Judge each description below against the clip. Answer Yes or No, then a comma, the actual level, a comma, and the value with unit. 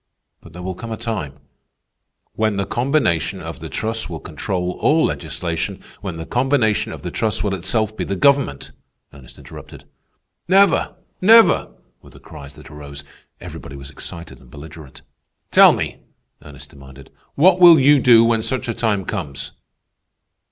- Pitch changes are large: Yes, wide, 8.3 semitones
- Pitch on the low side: Yes, low, 100 Hz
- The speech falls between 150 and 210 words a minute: Yes, average, 160 wpm